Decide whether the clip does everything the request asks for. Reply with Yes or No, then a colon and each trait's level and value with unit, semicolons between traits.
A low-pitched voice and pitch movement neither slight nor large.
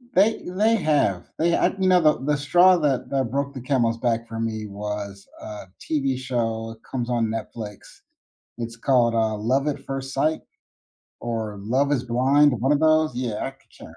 Yes: low, 125 Hz; average, 4.3 semitones